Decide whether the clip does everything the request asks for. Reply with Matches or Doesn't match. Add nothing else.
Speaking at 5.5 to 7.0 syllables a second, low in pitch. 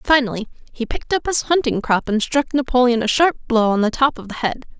Doesn't match